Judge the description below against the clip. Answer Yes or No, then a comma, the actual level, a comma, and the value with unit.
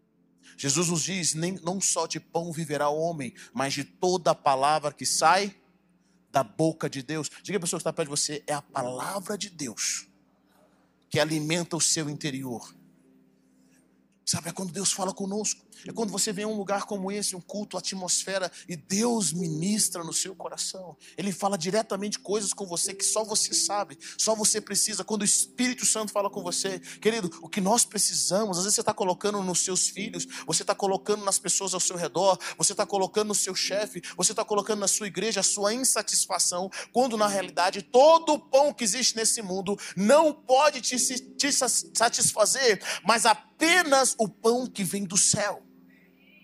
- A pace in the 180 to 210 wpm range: Yes, fast, 185 wpm